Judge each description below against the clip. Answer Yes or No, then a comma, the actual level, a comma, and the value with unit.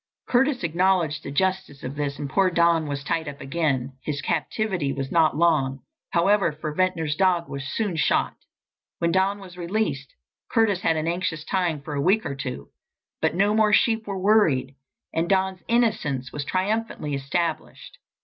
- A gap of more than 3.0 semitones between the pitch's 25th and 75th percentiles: Yes, average, 4.9 semitones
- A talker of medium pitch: Yes, medium, 170 Hz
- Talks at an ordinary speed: Yes, average, 170 wpm